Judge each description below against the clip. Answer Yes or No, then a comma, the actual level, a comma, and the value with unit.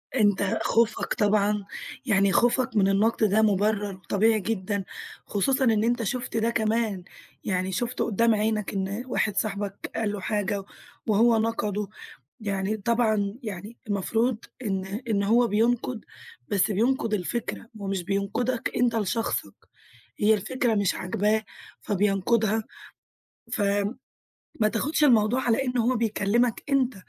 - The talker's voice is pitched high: Yes, high, 215 Hz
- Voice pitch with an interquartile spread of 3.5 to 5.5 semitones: No, narrow, 2.6 semitones